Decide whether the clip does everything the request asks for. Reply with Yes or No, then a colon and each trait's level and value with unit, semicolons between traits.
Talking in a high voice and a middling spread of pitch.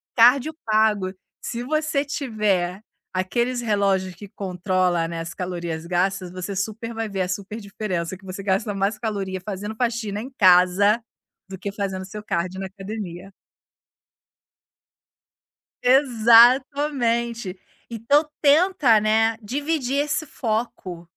Yes: high, 210 Hz; average, 4.1 semitones